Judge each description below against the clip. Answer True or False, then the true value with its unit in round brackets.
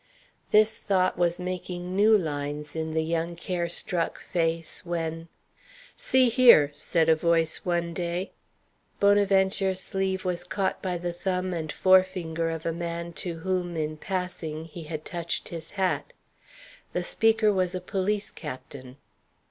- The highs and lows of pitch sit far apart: False (2.4 semitones)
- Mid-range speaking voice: True (175 Hz)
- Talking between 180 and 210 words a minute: False (145 wpm)